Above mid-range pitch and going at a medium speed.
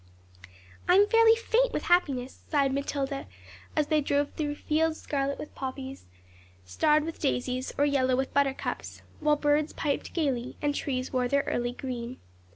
Yes: very high, 280 Hz; average, 160 wpm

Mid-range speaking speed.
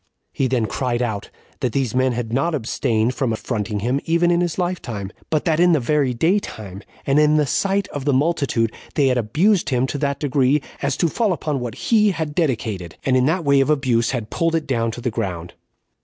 No: fast, 220 wpm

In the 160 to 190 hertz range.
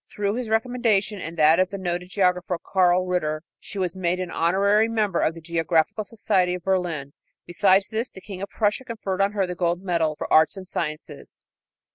Yes: medium, 185 Hz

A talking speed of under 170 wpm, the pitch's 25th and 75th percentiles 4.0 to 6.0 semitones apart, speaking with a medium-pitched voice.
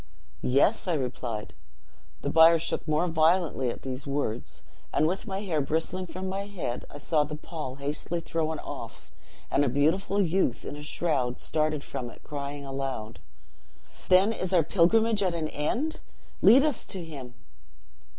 Yes: average, 160 wpm; average, 4.8 semitones; medium, 155 Hz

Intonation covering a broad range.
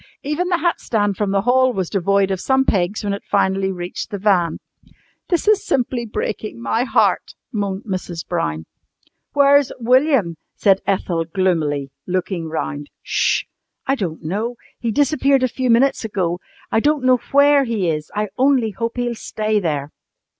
Yes: wide, 6.1 semitones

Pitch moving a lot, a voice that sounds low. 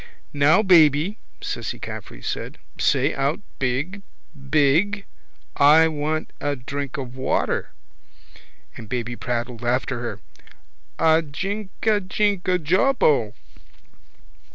No: wide, 5.8 semitones; medium, 150 Hz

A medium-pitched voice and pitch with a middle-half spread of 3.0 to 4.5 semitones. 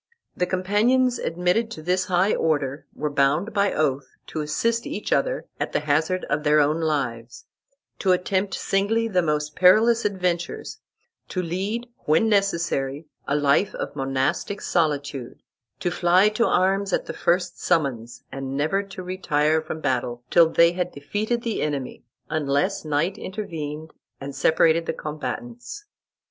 No: medium, 170 Hz; average, 5.0 semitones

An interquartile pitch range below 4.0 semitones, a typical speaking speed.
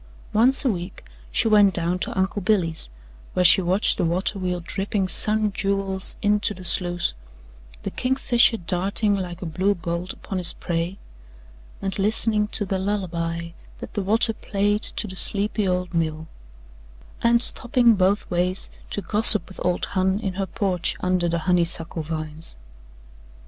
Yes: average, 2.9 semitones; average, 155 wpm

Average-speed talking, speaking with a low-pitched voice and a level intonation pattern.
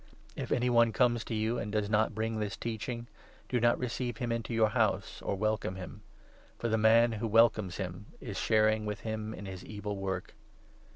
No: fast, 210 wpm; low, 110 Hz; narrow, 2.0 semitones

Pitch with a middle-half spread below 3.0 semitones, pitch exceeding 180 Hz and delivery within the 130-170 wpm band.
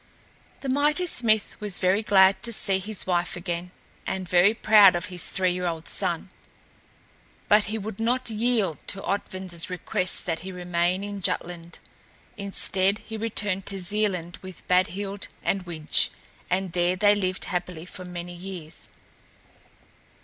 Yes: narrow, 2.5 semitones; high, 190 Hz; average, 150 wpm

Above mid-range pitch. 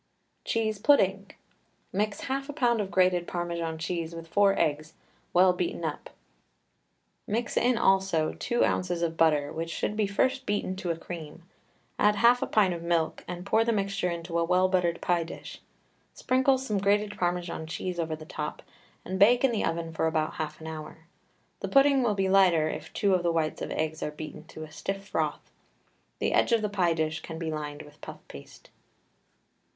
No: medium, 180 Hz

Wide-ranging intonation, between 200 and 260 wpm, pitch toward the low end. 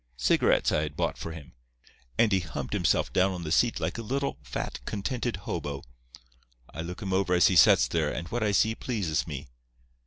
Yes: wide, 5.7 semitones; fast, 205 wpm; very low, 90 Hz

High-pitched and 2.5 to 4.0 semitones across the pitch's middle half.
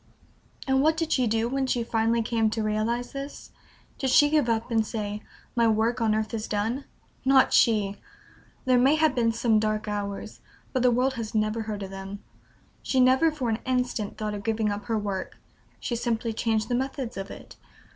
Yes: high, 230 Hz; average, 3.0 semitones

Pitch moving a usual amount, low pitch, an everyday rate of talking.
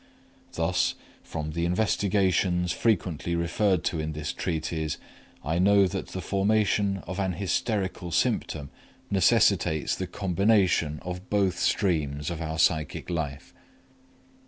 No: average, 3.5 semitones; very low, 90 Hz; slow, 120 wpm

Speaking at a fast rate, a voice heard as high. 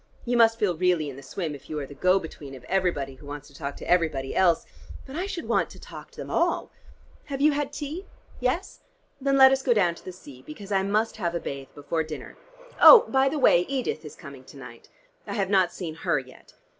No: fast, 240 wpm; medium, 180 Hz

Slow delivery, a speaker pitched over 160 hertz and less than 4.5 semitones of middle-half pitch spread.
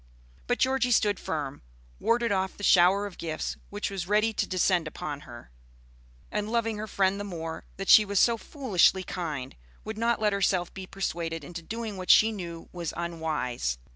No: average, 180 wpm; high, 190 Hz; average, 4.1 semitones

